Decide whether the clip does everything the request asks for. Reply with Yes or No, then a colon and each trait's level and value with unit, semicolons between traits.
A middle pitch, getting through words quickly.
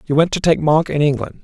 Yes: medium, 155 Hz; fast, 290 wpm